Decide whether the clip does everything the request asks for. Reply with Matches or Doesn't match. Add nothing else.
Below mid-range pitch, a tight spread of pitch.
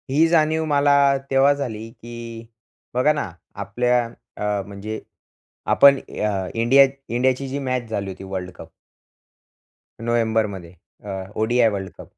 Doesn't match